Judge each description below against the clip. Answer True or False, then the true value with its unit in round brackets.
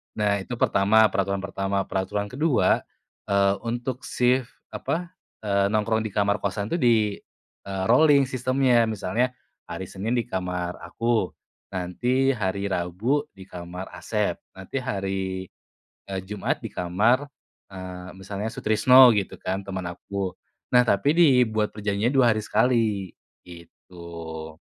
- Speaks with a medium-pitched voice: False (100 Hz)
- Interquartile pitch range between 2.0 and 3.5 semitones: False (4.3 semitones)